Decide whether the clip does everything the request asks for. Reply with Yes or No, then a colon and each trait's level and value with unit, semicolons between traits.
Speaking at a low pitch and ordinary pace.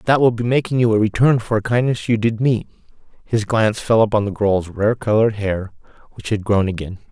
No: low, 110 Hz; fast, 220 wpm